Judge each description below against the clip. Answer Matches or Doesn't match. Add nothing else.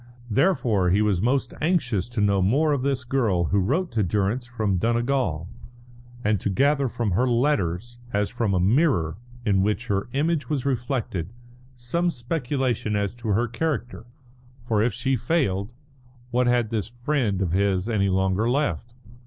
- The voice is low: Matches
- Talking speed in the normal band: Matches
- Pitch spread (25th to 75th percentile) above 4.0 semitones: Matches